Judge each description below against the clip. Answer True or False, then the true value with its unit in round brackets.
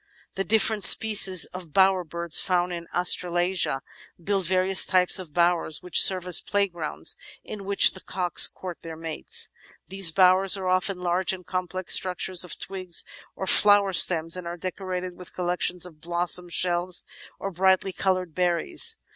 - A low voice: False (180 Hz)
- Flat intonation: True (1.5 semitones)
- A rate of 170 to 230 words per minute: False (155 wpm)